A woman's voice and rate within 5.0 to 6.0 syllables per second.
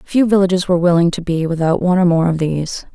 No: female; 6.7 syllables/s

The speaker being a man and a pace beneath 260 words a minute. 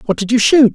No: male; fast, 325 wpm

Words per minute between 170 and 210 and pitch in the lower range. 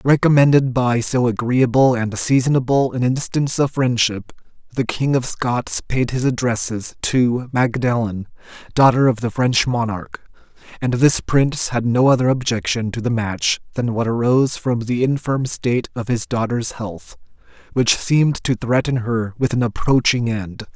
No: average, 155 wpm; low, 120 Hz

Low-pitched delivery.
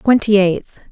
No: high, 205 Hz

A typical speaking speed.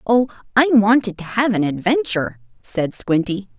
Yes: average, 150 wpm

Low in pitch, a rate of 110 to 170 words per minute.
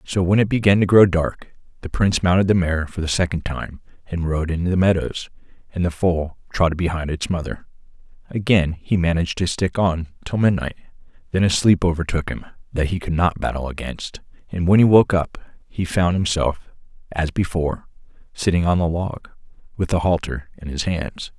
No: very low, 85 Hz; average, 190 wpm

